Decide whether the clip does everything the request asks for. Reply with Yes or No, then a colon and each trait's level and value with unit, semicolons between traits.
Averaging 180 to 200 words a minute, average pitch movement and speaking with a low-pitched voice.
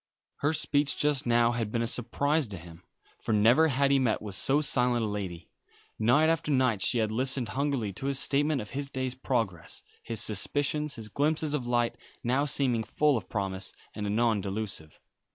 Yes: average, 190 wpm; average, 4.7 semitones; low, 120 Hz